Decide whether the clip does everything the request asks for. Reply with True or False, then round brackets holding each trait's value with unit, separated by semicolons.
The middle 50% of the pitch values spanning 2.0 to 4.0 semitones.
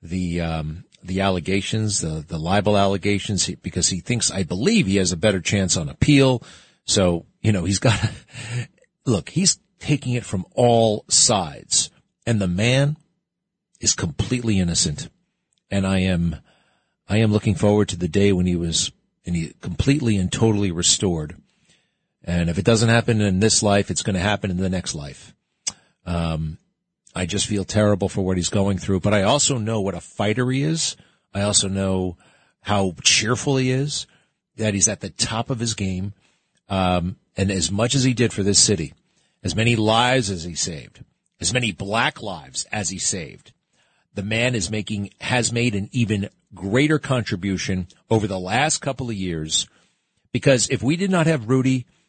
False (4.6 semitones)